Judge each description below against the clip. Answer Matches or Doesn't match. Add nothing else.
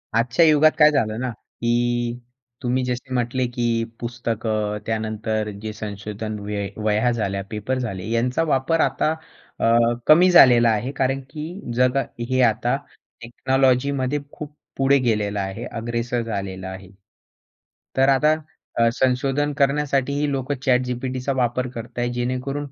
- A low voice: Matches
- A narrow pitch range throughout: Doesn't match